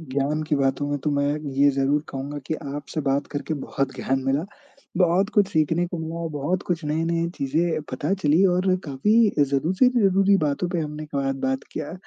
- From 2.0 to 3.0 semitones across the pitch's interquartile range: No, average, 3.5 semitones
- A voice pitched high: No, medium, 155 Hz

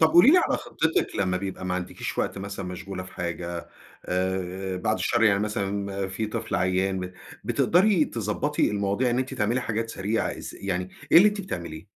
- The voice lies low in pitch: Yes, low, 100 Hz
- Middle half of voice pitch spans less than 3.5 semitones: No, average, 4.0 semitones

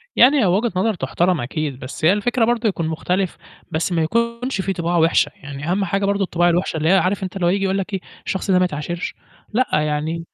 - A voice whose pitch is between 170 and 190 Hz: Yes, medium, 185 Hz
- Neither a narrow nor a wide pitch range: Yes, average, 3.5 semitones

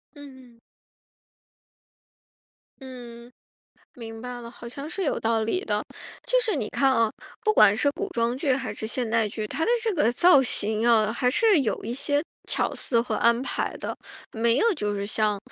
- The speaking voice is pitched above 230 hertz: Yes, high, 240 Hz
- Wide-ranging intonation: No, average, 4.1 semitones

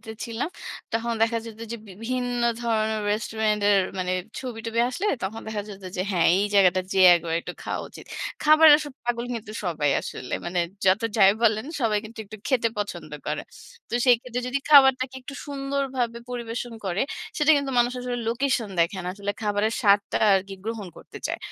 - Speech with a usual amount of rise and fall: Yes, average, 3.6 semitones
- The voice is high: Yes, high, 225 Hz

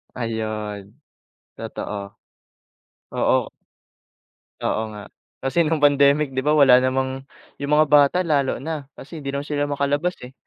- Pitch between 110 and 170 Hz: Yes, medium, 140 Hz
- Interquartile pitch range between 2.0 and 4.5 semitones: Yes, average, 2.9 semitones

